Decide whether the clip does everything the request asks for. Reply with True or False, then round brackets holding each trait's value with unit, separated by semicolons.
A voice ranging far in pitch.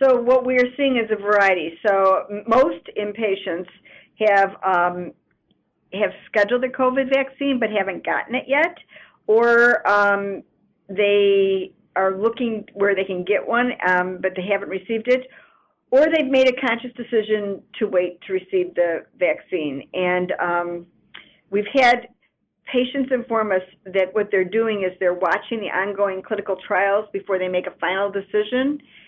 False (4.3 semitones)